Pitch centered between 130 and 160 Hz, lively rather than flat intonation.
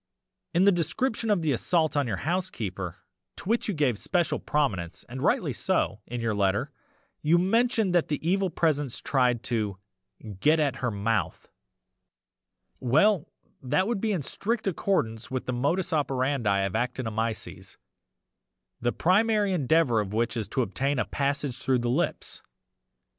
Yes: medium, 140 Hz; wide, 7.2 semitones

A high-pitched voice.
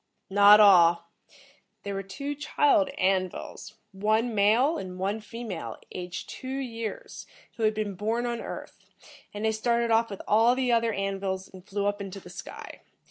Yes: high, 210 Hz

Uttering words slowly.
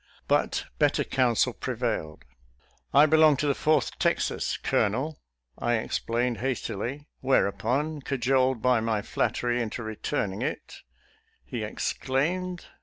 Yes: slow, 130 wpm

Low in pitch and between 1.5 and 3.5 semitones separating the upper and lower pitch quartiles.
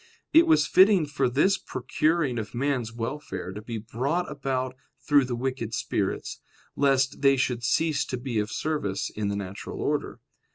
No: low, 130 Hz; average, 4.2 semitones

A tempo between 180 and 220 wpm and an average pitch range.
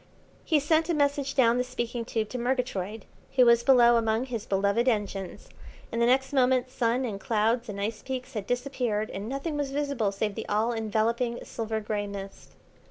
Yes: average, 185 wpm; average, 3.2 semitones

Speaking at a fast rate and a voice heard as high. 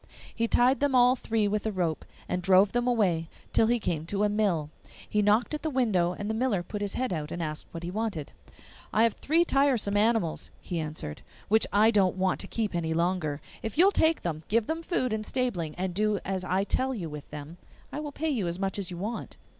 Yes: fast, 235 wpm; high, 205 Hz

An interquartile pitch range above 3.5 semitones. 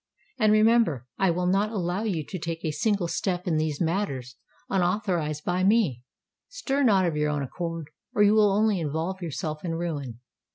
Yes: average, 4.8 semitones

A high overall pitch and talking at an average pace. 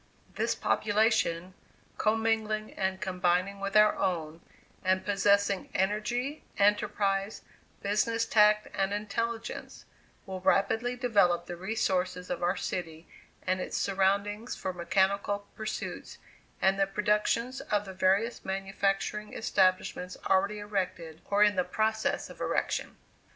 No: high, 200 Hz; slow, 115 wpm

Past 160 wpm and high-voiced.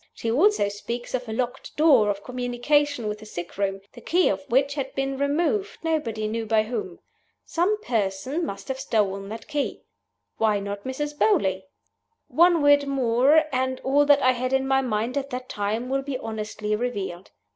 Yes: average, 180 wpm; very high, 250 Hz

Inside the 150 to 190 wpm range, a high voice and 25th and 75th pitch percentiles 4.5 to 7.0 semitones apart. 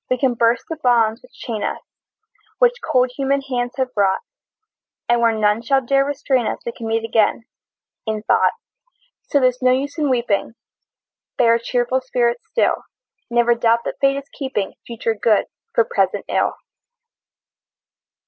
No: average, 160 wpm; high, 245 Hz; average, 2.8 semitones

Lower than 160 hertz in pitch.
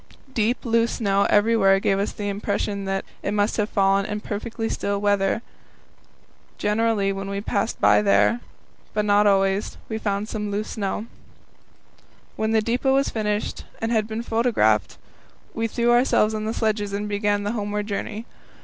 No: high, 210 Hz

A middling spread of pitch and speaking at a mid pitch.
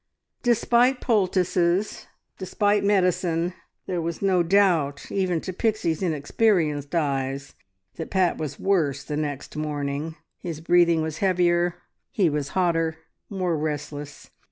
Yes: average, 3.7 semitones; medium, 170 Hz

